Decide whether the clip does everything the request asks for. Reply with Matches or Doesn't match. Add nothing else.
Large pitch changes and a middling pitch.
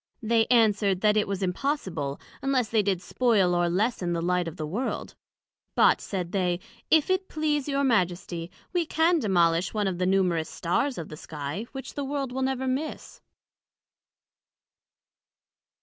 Doesn't match